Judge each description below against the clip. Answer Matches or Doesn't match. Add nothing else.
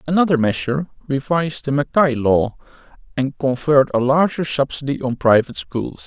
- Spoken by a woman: Doesn't match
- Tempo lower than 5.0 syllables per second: Doesn't match